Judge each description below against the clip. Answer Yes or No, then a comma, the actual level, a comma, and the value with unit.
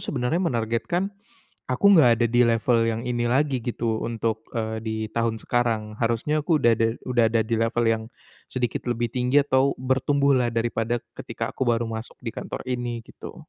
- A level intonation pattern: Yes, narrow, 1.9 semitones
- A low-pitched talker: Yes, low, 120 Hz